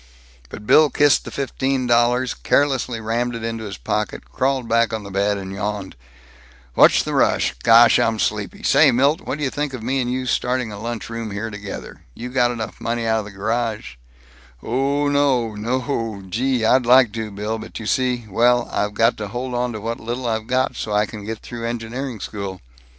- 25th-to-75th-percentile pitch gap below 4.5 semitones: Yes, average, 3.0 semitones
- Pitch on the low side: Yes, low, 115 Hz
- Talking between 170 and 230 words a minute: Yes, average, 195 wpm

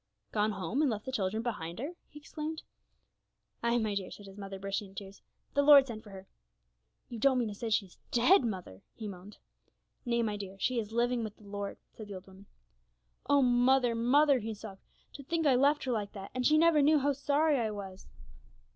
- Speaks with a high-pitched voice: Yes, high, 225 Hz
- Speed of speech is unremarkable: No, fast, 215 wpm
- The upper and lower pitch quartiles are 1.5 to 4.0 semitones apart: No, average, 5.1 semitones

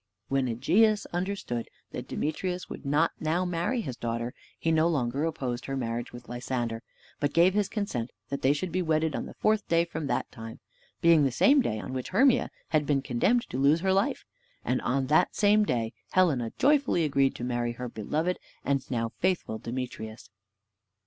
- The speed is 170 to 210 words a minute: Yes, average, 185 wpm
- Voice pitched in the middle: Yes, medium, 145 Hz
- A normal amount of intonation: No, wide, 6.6 semitones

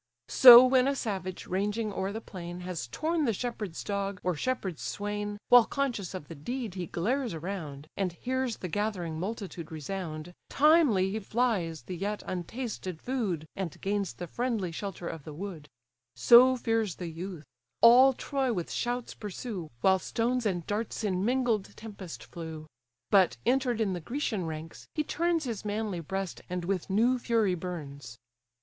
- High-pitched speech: Yes, high, 200 Hz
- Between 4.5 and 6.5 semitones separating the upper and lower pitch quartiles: Yes, average, 5.2 semitones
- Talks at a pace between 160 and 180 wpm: Yes, average, 165 wpm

